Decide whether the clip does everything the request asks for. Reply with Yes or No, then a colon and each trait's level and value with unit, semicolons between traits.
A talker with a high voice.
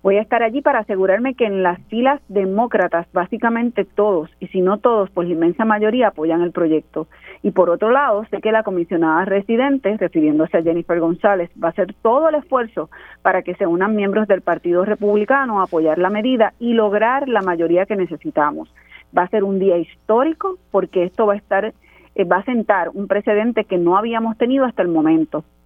Yes: high, 195 Hz